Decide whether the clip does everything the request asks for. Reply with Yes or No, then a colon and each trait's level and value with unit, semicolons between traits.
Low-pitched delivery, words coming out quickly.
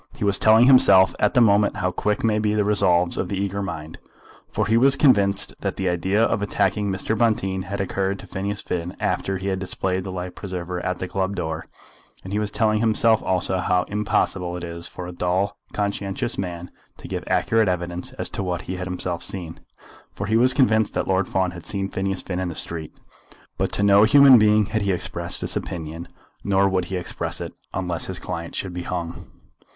Yes: very low, 95 Hz; fast, 210 wpm